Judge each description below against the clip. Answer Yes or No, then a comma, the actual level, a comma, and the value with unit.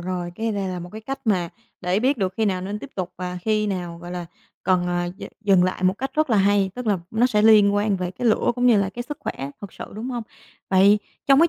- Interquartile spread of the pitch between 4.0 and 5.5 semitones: No, average, 3.4 semitones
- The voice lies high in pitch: Yes, high, 200 Hz